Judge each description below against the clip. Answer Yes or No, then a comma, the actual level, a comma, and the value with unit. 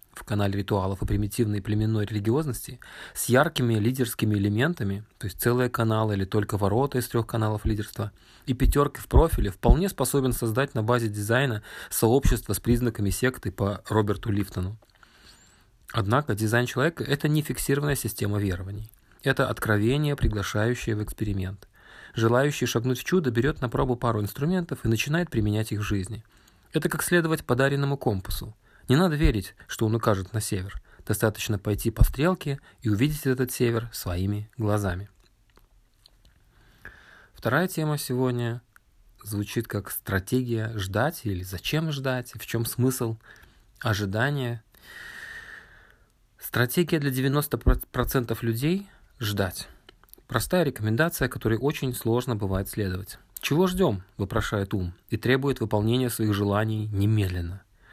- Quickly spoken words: No, average, 130 wpm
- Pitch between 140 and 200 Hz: No, low, 115 Hz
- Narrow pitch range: No, average, 3.8 semitones